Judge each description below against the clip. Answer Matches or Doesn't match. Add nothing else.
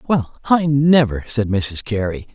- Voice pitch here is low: Matches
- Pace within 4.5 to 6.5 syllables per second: Doesn't match